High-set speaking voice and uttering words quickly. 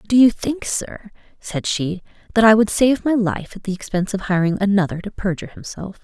Yes: high, 205 Hz; fast, 220 wpm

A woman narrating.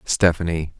No: male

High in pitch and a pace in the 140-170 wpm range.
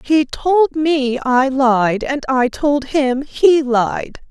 Yes: very high, 275 Hz; average, 155 wpm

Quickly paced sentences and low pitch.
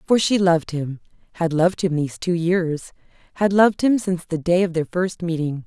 No: fast, 210 wpm; medium, 175 Hz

